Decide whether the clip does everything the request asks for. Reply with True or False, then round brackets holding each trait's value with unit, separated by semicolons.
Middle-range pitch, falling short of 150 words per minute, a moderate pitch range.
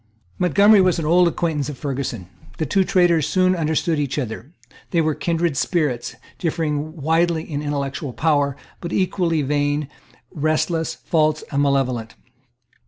True (155 Hz; 140 wpm; 3.1 semitones)